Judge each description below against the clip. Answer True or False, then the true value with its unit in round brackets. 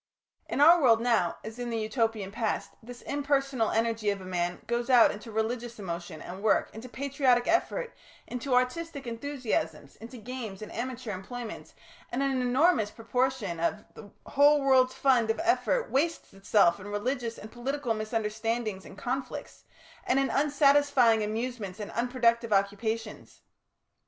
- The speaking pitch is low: False (235 Hz)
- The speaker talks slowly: False (150 wpm)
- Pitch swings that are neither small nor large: True (3.6 semitones)